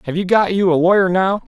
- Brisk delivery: Yes, fast, 270 wpm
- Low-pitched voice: No, medium, 185 Hz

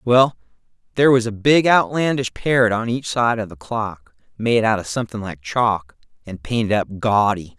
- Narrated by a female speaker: No, male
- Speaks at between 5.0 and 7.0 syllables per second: No, 4.8 syllables/s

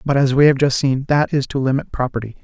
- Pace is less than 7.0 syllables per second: Yes, 6.3 syllables/s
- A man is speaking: Yes, male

